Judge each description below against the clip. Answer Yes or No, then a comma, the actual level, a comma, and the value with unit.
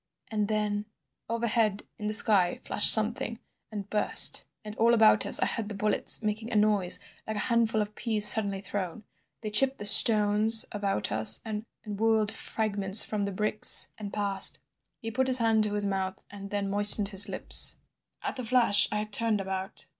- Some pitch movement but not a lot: No, narrow, 1.6 semitones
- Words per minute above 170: Yes, average, 185 wpm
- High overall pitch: Yes, high, 210 Hz